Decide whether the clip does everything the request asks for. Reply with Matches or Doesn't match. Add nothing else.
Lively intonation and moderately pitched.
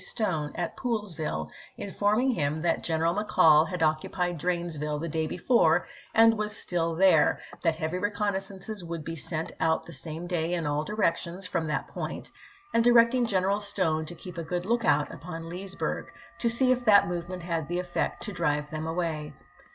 Doesn't match